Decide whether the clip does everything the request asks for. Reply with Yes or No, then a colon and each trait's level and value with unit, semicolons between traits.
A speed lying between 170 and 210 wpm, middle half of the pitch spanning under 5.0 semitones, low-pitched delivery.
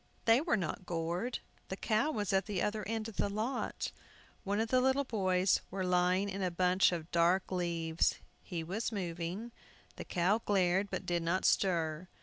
No: average, 180 wpm; average, 3.6 semitones; high, 190 Hz